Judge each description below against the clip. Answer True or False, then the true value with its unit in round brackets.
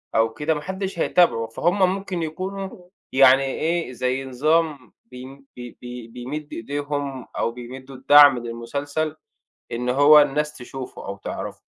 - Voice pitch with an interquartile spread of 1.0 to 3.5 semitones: False (4.1 semitones)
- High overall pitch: False (140 Hz)